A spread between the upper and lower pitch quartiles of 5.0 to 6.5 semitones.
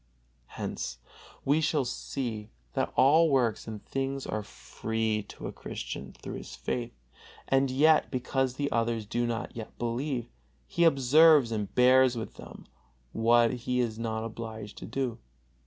No: average, 3.1 semitones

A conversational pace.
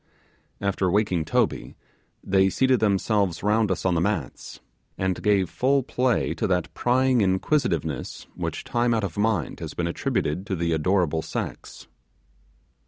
Yes: average, 145 wpm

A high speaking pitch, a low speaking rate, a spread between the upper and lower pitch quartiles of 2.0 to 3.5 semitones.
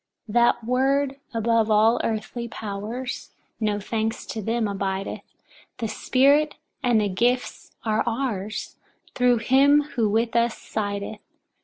Yes: high, 230 Hz; slow, 130 wpm; narrow, 2.5 semitones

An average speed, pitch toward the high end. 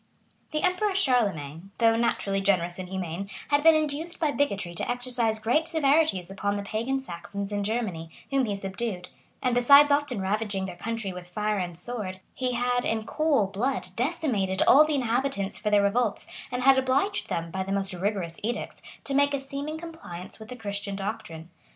Yes: average, 180 wpm; high, 220 Hz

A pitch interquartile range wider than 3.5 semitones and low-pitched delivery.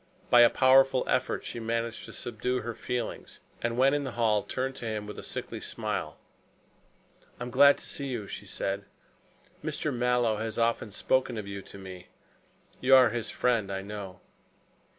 No: average, 3.2 semitones; low, 120 Hz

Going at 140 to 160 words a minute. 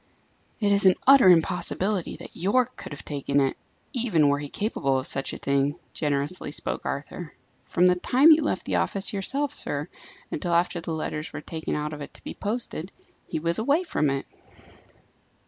No: average, 185 wpm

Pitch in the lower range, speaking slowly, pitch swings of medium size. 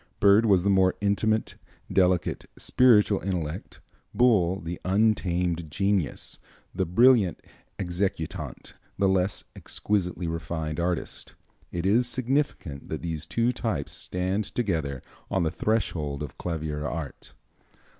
Yes: very low, 95 Hz; slow, 115 wpm; average, 4.0 semitones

